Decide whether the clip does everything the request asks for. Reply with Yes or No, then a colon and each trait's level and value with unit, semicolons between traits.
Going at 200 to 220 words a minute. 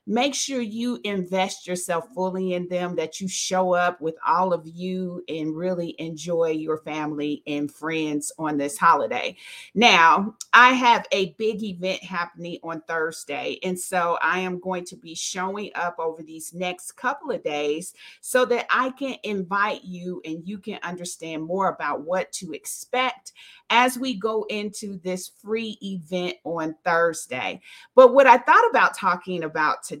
No: average, 165 wpm